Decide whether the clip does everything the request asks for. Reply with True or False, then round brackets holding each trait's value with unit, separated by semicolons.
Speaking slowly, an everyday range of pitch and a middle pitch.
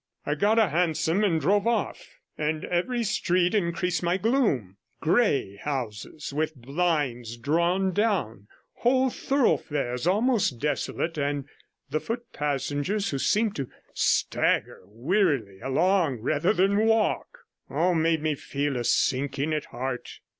False (130 wpm; 6.4 semitones; 160 Hz)